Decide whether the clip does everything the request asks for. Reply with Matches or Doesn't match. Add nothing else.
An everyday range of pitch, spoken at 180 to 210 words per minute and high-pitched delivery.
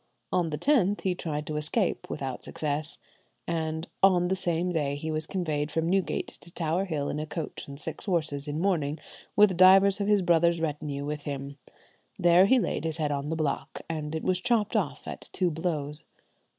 Doesn't match